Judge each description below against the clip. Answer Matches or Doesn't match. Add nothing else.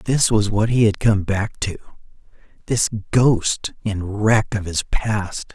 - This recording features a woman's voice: Doesn't match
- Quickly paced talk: Doesn't match